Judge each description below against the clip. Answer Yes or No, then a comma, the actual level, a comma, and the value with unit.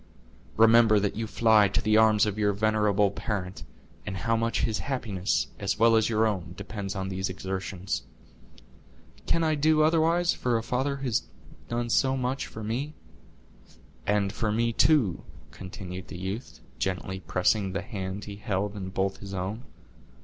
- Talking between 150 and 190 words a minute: Yes, average, 165 wpm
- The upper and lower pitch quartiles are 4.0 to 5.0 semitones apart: No, average, 3.3 semitones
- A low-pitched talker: Yes, low, 105 Hz